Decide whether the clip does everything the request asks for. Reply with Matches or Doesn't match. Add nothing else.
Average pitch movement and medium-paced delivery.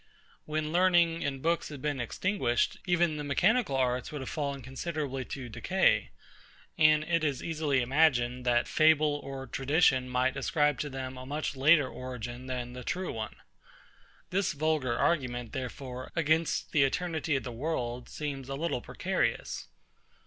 Matches